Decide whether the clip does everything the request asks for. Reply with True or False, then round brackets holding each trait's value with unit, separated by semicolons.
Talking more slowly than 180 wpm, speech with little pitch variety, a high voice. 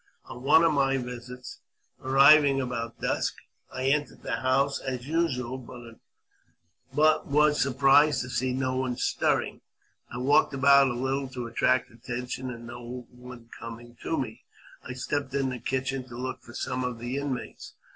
False (160 wpm; 1.9 semitones; 130 Hz)